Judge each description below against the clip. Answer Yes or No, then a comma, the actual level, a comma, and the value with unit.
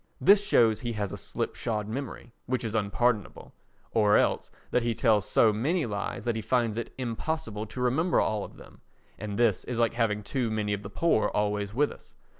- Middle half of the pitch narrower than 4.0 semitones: Yes, average, 2.9 semitones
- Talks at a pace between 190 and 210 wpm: Yes, average, 200 wpm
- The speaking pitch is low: Yes, low, 115 Hz